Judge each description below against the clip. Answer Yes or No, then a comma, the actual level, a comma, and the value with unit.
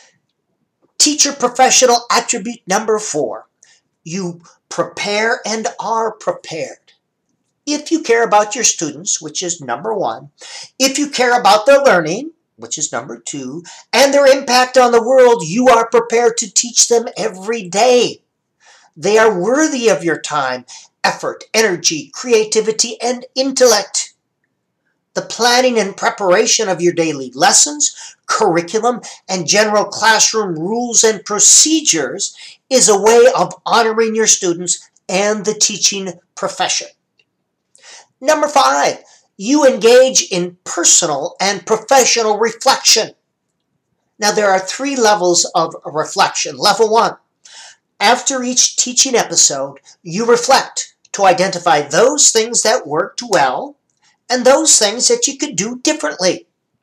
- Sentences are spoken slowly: Yes, slow, 125 wpm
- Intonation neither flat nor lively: Yes, average, 4.8 semitones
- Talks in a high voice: Yes, high, 225 Hz